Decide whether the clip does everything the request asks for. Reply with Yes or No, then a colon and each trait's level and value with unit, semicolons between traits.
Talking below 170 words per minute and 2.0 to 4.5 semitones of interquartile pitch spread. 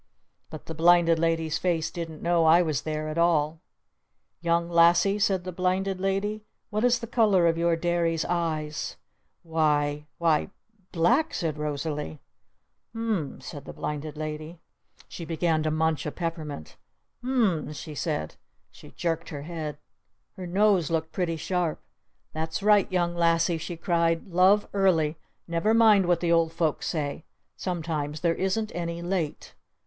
Yes: average, 160 wpm; narrow, 2.6 semitones